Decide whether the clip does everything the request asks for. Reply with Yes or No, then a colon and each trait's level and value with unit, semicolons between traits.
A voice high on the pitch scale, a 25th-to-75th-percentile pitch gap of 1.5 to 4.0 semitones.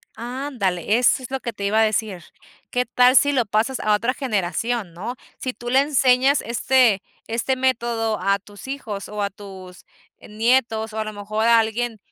Yes: high, 225 Hz; average, 3.3 semitones